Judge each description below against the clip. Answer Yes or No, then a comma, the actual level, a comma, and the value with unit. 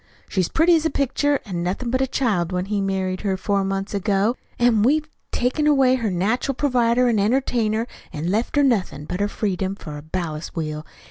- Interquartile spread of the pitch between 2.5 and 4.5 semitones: No, average, 5.3 semitones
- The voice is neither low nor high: No, high, 210 Hz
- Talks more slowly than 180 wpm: No, average, 200 wpm